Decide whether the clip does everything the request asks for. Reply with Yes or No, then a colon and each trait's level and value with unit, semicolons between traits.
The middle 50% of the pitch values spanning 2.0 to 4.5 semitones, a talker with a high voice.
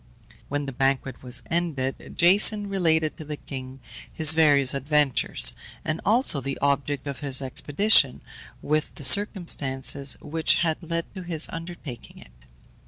No: average, 3.7 semitones; medium, 150 Hz